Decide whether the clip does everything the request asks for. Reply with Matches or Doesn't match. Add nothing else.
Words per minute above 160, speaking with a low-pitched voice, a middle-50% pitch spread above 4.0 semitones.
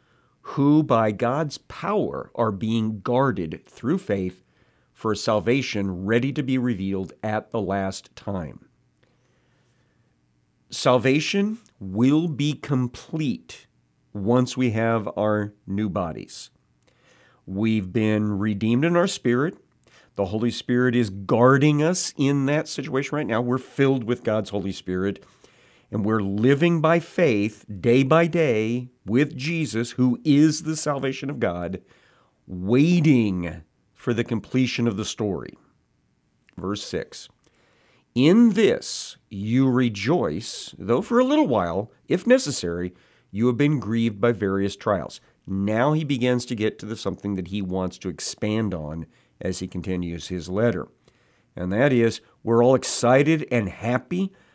Doesn't match